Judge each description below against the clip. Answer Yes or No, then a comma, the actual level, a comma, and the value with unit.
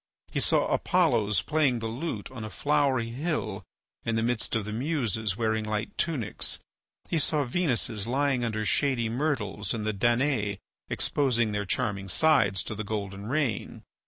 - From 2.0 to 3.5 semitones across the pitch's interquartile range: No, average, 4.6 semitones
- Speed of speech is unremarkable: Yes, average, 160 wpm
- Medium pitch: No, low, 115 Hz